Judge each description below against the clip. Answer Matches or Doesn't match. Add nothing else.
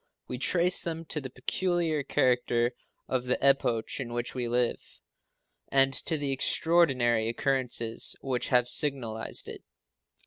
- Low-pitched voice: Matches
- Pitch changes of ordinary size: Matches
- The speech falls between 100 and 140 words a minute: Matches